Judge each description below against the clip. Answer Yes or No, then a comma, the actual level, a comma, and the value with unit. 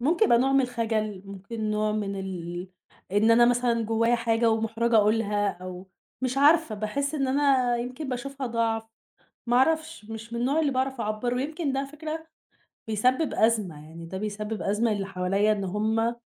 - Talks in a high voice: Yes, high, 230 Hz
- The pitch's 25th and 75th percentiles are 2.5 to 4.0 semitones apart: Yes, average, 3.7 semitones